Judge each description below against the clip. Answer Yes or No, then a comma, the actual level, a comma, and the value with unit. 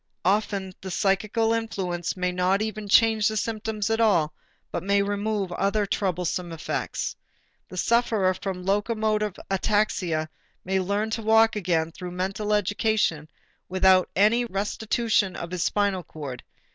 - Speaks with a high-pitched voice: Yes, high, 200 Hz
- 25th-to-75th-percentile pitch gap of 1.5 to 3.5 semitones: Yes, average, 3.0 semitones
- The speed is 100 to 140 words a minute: Yes, slow, 135 wpm